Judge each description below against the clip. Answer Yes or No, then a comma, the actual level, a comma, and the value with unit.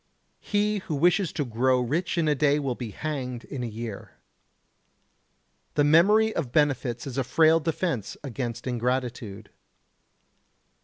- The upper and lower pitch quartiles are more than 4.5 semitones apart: Yes, average, 5.0 semitones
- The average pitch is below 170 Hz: Yes, low, 135 Hz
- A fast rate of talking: No, average, 140 wpm